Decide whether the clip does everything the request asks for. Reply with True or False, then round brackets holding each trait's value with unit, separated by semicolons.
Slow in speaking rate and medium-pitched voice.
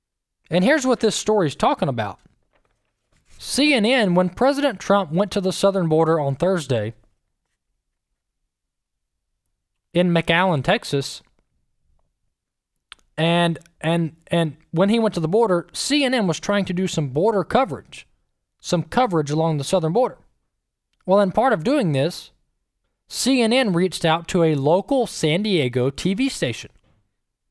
True (130 wpm; 175 Hz)